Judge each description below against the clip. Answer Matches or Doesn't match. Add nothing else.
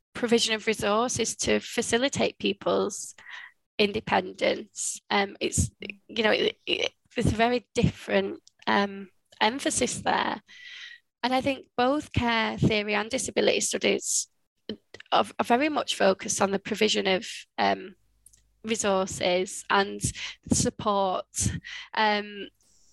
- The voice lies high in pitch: Matches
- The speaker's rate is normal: Doesn't match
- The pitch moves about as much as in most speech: Matches